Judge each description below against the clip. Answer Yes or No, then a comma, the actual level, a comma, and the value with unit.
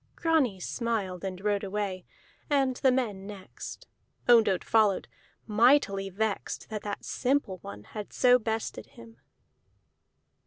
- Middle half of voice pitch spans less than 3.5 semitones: No, average, 4.0 semitones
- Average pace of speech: No, slow, 120 wpm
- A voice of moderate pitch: No, high, 215 Hz